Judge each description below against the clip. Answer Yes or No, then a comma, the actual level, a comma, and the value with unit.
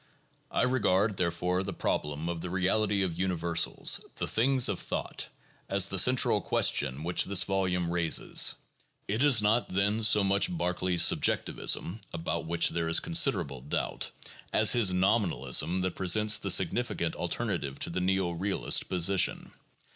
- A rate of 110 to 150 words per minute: No, average, 160 wpm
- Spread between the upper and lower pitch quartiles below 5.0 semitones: Yes, average, 3.3 semitones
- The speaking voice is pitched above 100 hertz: No, very low, 95 Hz